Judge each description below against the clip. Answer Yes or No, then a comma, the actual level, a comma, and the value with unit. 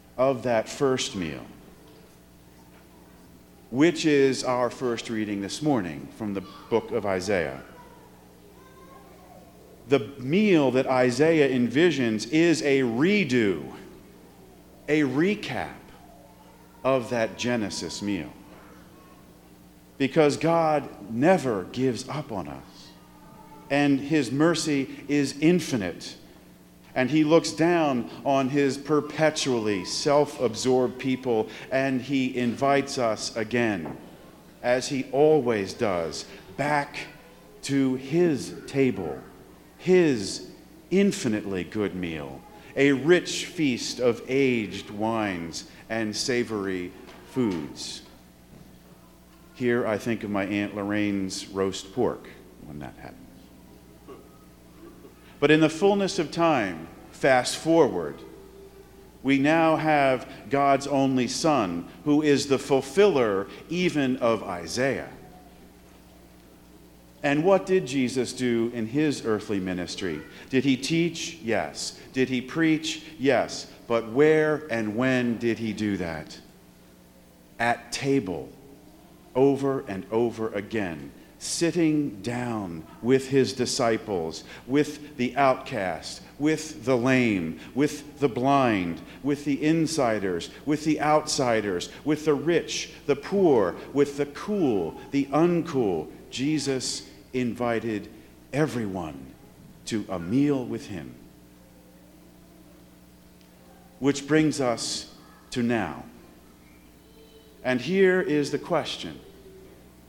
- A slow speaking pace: Yes, slow, 105 wpm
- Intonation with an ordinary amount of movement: No, wide, 7.3 semitones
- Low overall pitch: Yes, low, 125 Hz